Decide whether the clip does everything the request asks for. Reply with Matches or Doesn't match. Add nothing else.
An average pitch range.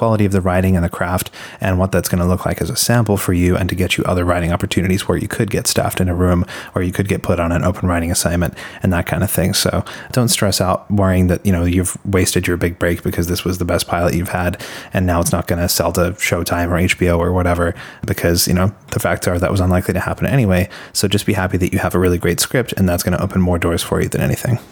Doesn't match